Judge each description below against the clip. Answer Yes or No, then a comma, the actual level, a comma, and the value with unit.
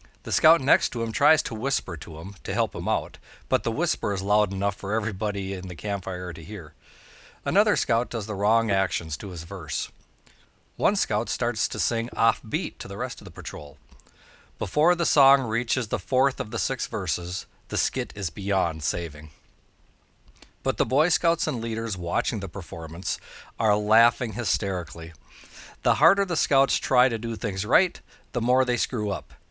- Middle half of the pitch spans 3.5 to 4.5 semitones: No, average, 4.9 semitones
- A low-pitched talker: Yes, low, 105 Hz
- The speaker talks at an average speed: Yes, average, 185 wpm